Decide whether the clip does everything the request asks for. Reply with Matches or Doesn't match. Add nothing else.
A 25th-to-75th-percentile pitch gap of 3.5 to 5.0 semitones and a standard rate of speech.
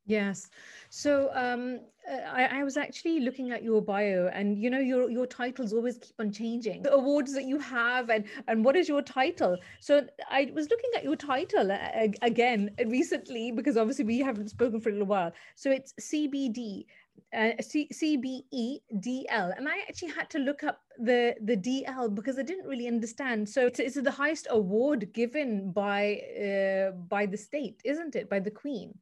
Matches